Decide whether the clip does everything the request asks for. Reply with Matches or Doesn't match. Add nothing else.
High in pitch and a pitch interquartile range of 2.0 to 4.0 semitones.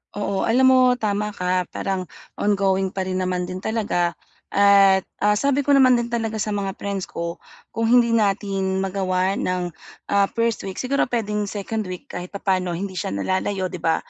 Matches